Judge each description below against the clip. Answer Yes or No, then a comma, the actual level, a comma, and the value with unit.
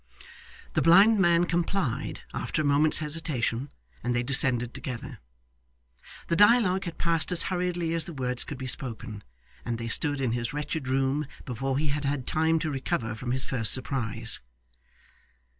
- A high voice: No, medium, 140 Hz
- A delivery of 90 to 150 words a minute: No, average, 160 wpm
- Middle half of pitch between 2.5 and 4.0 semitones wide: No, average, 5.1 semitones